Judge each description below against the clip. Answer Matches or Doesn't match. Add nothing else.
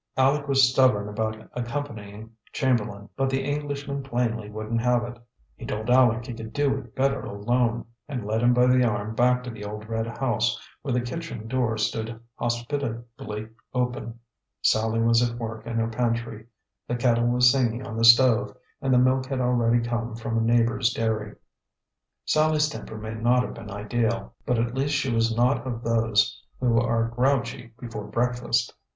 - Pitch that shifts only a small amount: Matches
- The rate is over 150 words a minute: Matches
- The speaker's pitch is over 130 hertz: Doesn't match